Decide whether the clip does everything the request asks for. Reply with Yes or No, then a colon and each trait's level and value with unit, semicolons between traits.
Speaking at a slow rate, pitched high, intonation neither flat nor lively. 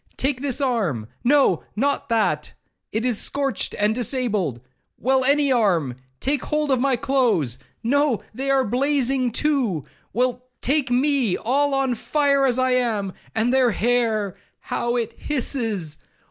Yes: slow, 120 wpm; high, 245 Hz; average, 4.2 semitones